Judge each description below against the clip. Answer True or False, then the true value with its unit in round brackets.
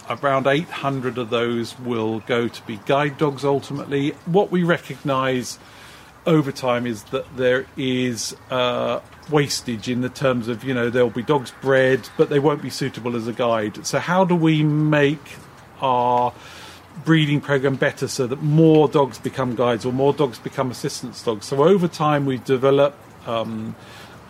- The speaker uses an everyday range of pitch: True (3.0 semitones)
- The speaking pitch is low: True (130 Hz)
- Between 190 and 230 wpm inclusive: False (165 wpm)